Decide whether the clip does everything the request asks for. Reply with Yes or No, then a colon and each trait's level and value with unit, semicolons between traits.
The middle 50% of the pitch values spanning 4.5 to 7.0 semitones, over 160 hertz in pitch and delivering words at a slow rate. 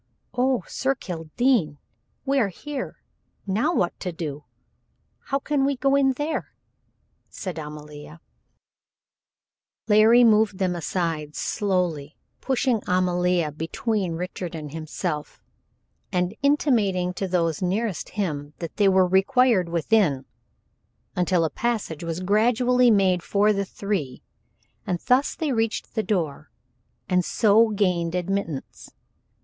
Yes: wide, 5.4 semitones; high, 190 Hz; slow, 120 wpm